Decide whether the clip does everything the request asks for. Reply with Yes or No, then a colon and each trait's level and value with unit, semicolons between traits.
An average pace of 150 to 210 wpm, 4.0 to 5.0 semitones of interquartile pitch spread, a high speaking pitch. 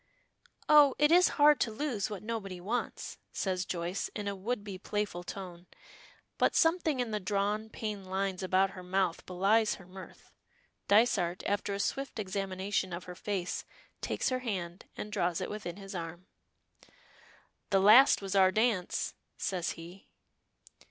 No: average, 155 wpm; average, 2.9 semitones; high, 195 Hz